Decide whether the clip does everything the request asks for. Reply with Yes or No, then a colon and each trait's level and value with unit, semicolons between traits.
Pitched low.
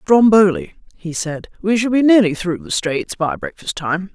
No: high, 195 Hz